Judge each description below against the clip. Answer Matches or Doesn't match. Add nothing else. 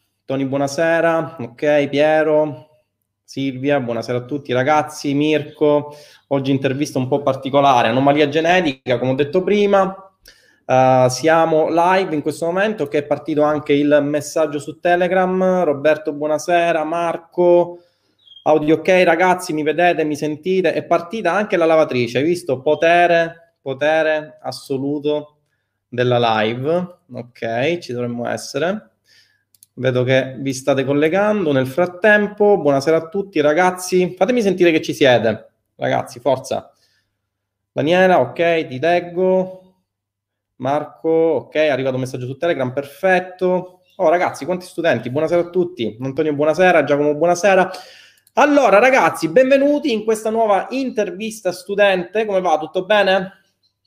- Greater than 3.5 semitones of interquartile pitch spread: Matches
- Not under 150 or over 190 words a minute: Doesn't match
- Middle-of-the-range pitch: Matches